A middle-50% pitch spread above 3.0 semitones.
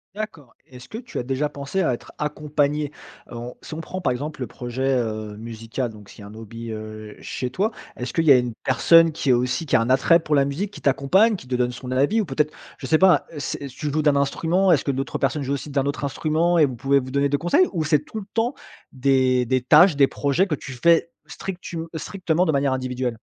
Yes: average, 4.3 semitones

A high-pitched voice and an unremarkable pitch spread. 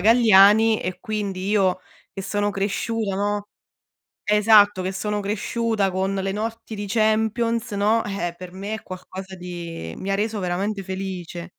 No: high, 200 Hz; narrow, 2.3 semitones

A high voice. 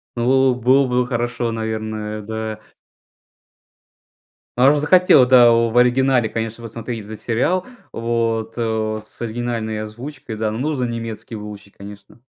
No: low, 115 Hz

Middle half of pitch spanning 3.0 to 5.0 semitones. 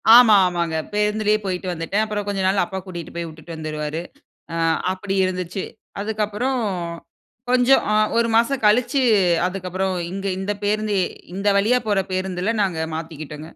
Yes: average, 3.5 semitones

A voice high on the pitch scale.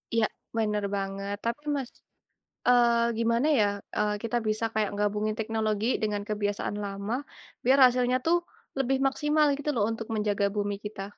Yes: high, 220 Hz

